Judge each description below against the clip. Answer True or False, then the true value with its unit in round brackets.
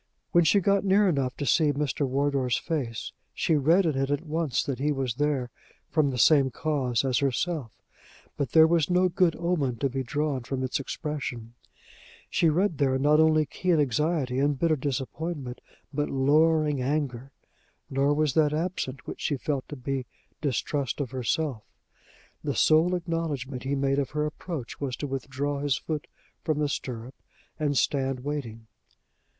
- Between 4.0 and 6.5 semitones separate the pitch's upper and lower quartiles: False (2.9 semitones)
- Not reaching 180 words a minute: True (165 wpm)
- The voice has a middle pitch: True (145 Hz)